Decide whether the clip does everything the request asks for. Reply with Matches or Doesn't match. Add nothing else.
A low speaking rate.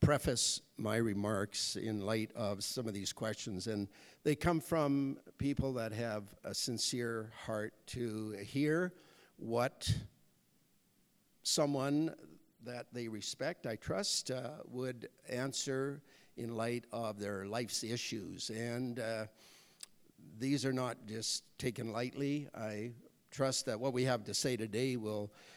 Matches